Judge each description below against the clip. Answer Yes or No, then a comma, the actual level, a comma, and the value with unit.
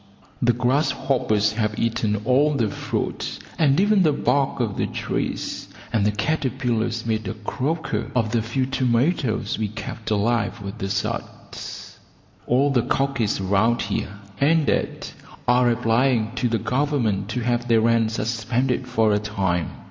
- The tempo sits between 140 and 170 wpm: Yes, average, 150 wpm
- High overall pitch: No, low, 115 Hz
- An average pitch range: Yes, average, 3.3 semitones